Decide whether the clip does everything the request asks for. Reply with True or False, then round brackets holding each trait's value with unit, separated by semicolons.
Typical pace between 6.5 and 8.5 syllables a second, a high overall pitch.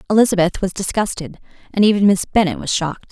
True (6.6 syllables/s; 195 Hz)